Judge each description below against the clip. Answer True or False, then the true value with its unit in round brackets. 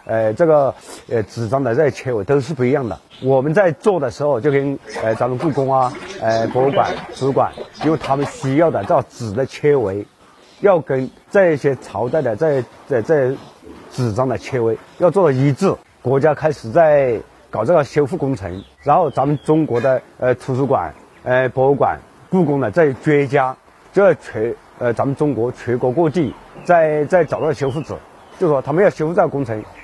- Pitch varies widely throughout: False (3.6 semitones)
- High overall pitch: False (135 Hz)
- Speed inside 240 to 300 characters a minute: True (265 characters per minute)